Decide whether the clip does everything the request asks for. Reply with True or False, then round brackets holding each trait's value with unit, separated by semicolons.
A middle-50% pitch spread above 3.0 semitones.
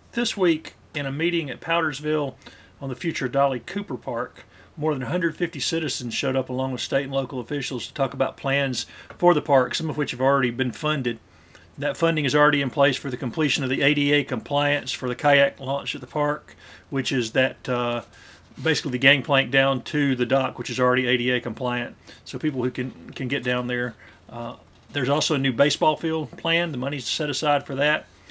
False (2.7 semitones)